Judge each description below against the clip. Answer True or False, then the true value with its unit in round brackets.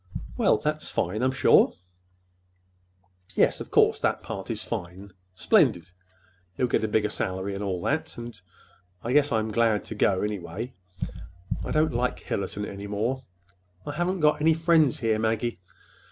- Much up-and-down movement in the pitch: False (4.6 semitones)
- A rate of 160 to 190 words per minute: False (150 wpm)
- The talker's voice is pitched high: False (110 Hz)